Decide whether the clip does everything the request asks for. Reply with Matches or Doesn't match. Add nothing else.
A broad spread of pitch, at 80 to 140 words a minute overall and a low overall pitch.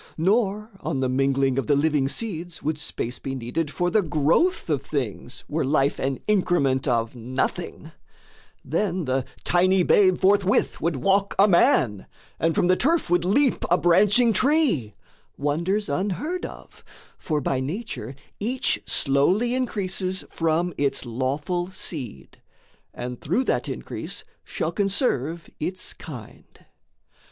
Doesn't match